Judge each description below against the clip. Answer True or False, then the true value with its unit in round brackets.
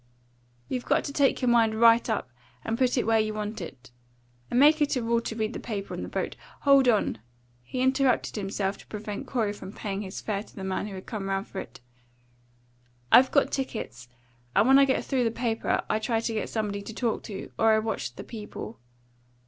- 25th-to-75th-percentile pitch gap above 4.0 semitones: False (3.4 semitones)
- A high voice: True (225 Hz)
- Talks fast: True (220 wpm)